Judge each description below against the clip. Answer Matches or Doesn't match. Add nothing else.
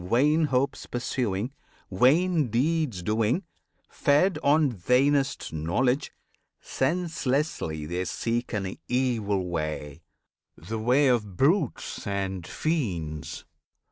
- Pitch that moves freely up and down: Matches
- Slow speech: Matches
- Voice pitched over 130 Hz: Doesn't match